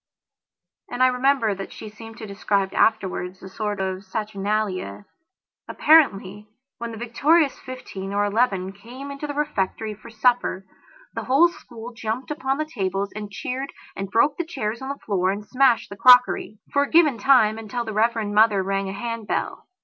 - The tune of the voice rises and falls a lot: No, average, 4.3 semitones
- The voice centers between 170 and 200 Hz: No, high, 220 Hz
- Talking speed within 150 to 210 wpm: Yes, average, 170 wpm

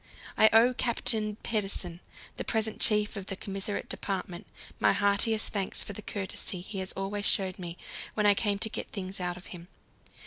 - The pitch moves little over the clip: Yes, narrow, 2.2 semitones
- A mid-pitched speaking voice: No, high, 200 Hz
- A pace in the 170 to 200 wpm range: Yes, average, 175 wpm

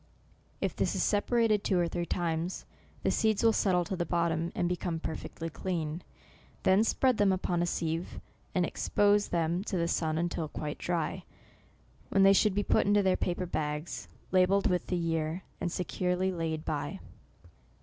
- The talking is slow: No, average, 170 wpm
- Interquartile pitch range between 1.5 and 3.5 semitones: Yes, narrow, 2.6 semitones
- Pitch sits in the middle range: Yes, medium, 175 Hz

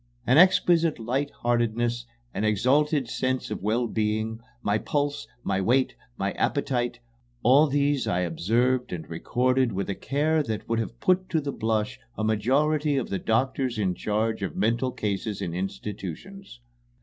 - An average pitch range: Yes, average, 4.6 semitones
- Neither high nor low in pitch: No, low, 120 Hz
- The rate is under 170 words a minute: Yes, average, 150 wpm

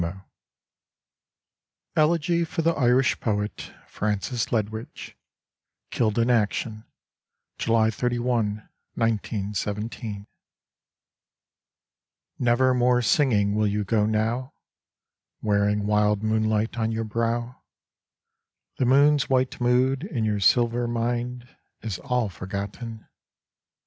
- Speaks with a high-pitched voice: No, low, 115 Hz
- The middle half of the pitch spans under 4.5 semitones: Yes, average, 2.8 semitones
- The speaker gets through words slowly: Yes, slow, 100 wpm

